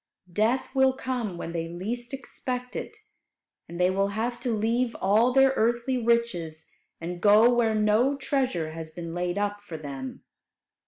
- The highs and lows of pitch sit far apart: Yes, wide, 5.9 semitones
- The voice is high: Yes, high, 220 Hz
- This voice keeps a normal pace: Yes, average, 160 wpm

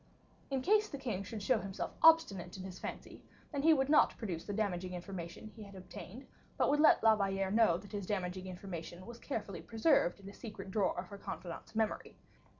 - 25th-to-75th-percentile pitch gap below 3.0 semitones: No, average, 4.0 semitones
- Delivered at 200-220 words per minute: Yes, fast, 205 wpm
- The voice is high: Yes, high, 200 Hz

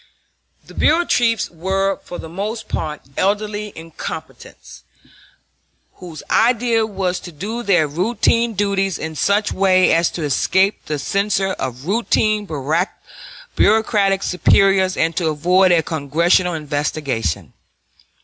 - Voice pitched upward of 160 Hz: Yes, high, 190 Hz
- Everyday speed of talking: No, slow, 120 wpm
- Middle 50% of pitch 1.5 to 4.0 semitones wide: No, average, 4.4 semitones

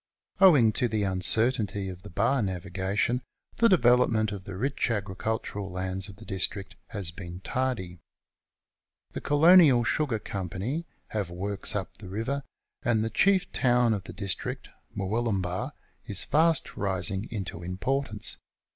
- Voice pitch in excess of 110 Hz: No, low, 105 Hz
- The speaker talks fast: No, average, 140 wpm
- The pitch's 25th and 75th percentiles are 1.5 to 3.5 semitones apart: No, average, 4.5 semitones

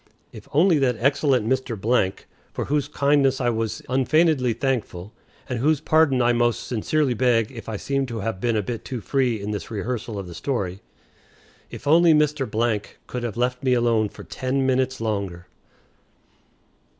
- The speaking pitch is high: No, low, 125 Hz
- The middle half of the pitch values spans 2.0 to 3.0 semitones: No, average, 3.6 semitones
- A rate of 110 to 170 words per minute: Yes, average, 165 wpm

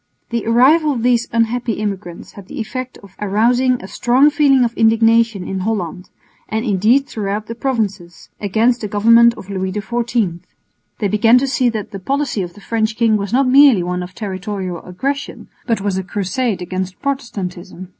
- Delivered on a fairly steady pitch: No, average, 4.0 semitones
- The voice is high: Yes, high, 220 Hz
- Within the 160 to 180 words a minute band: Yes, average, 175 wpm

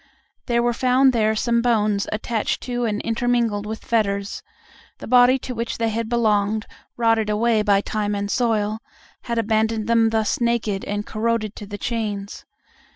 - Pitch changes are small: Yes, narrow, 2.0 semitones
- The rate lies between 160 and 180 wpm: Yes, average, 165 wpm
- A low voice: No, high, 225 Hz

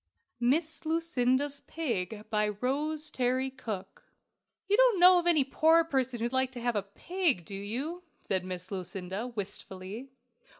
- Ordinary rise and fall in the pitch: No, wide, 7.4 semitones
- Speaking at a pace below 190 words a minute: Yes, average, 145 wpm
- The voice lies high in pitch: Yes, very high, 255 Hz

